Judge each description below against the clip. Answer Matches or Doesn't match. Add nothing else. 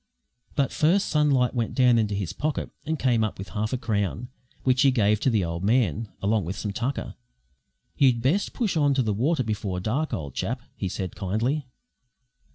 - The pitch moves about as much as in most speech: Matches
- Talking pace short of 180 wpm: Doesn't match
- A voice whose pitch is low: Matches